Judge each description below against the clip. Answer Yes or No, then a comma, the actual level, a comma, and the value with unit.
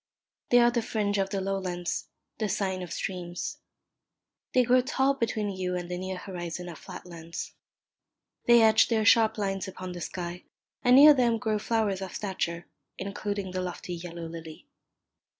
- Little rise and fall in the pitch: No, average, 3.7 semitones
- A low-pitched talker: No, high, 190 Hz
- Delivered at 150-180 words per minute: Yes, average, 170 wpm